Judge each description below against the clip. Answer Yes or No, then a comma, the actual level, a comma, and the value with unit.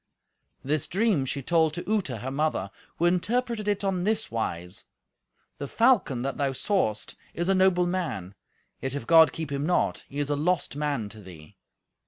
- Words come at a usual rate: Yes, average, 180 wpm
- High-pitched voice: No, medium, 155 Hz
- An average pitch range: No, wide, 6.0 semitones